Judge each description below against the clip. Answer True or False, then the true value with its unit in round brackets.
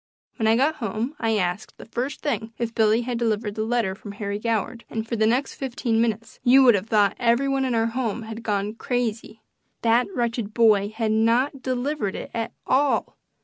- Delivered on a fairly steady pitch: True (2.1 semitones)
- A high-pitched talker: True (230 Hz)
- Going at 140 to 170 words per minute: False (200 wpm)